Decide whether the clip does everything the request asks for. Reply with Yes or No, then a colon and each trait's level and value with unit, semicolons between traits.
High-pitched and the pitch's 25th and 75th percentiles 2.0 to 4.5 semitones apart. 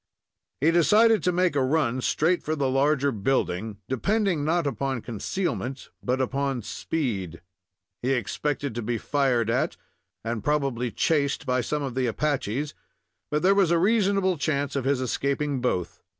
No: medium, 140 Hz; average, 4.0 semitones